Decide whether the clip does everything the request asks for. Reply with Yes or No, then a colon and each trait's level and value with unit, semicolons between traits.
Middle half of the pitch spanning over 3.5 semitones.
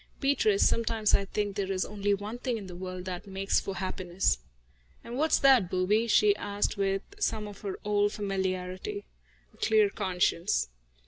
No: average, 2.7 semitones